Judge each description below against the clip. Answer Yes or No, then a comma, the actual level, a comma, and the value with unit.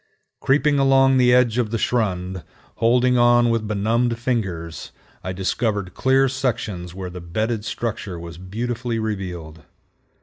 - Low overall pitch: Yes, low, 115 Hz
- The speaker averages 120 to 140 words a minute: Yes, slow, 135 wpm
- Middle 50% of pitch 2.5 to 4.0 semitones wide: No, average, 4.8 semitones